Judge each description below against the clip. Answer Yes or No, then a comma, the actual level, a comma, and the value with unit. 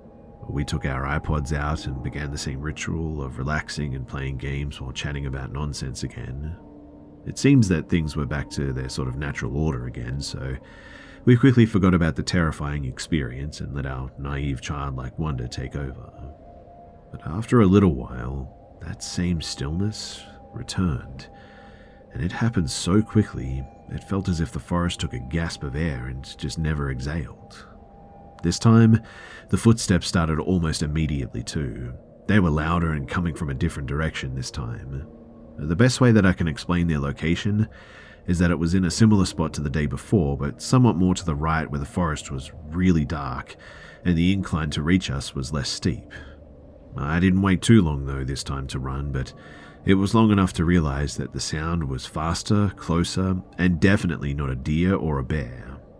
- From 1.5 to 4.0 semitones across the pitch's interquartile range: No, average, 4.7 semitones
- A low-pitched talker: Yes, very low, 80 Hz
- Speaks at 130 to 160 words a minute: No, average, 180 wpm